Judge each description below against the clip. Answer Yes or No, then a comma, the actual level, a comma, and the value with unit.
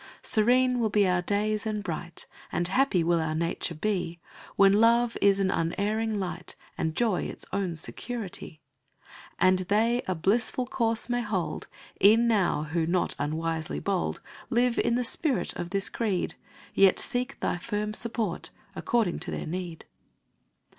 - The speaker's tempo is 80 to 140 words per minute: No, average, 155 wpm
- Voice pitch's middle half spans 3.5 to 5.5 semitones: Yes, average, 4.8 semitones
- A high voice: Yes, high, 200 Hz